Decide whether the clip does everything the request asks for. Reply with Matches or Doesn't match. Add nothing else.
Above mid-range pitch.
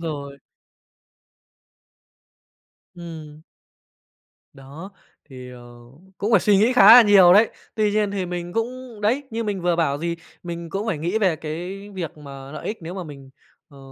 Doesn't match